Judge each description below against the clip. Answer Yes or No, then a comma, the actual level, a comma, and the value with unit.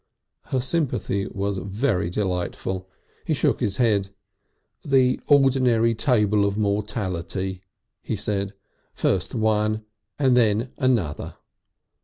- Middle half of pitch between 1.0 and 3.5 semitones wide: No, average, 4.1 semitones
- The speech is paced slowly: Yes, slow, 105 wpm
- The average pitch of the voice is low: Yes, low, 105 Hz